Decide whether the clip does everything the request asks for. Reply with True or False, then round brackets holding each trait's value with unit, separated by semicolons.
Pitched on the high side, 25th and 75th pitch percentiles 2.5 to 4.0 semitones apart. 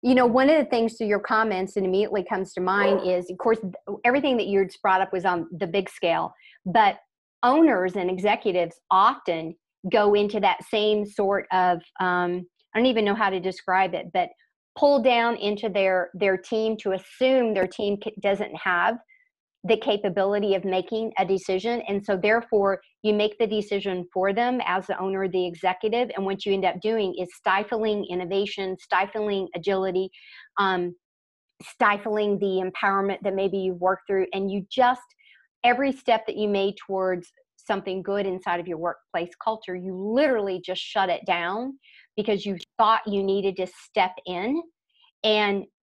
True (200 Hz; 2.9 semitones)